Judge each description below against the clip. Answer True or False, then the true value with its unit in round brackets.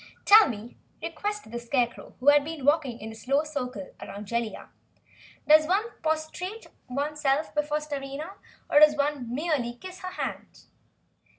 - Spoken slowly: False (155 wpm)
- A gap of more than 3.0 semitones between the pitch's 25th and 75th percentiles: True (4.1 semitones)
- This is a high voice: True (290 Hz)